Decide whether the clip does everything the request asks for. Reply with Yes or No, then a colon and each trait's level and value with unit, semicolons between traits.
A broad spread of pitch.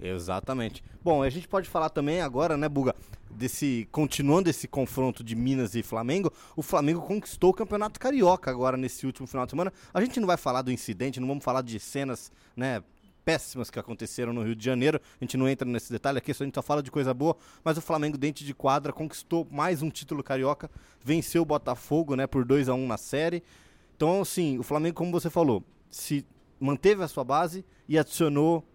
No: average, 4.3 semitones